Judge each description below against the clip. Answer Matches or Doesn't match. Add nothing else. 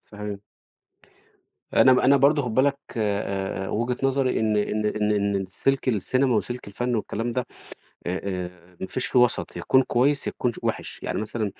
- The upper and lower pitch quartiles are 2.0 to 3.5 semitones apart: Doesn't match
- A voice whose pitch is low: Matches